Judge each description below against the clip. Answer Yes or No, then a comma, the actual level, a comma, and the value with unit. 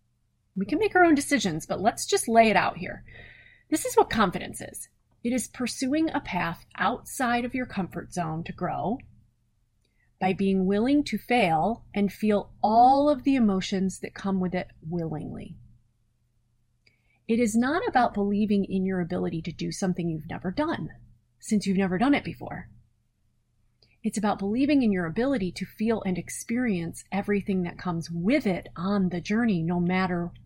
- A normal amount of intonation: No, wide, 5.8 semitones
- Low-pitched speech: No, high, 190 Hz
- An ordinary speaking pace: Yes, average, 170 wpm